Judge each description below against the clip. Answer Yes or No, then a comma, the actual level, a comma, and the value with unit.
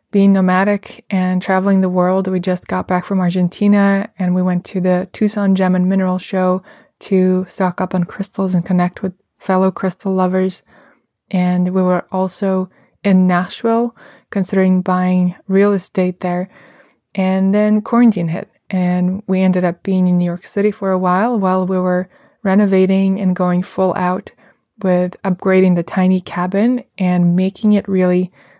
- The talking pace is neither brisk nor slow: Yes, average, 160 wpm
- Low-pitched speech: No, medium, 185 Hz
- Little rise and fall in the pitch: Yes, narrow, 1.2 semitones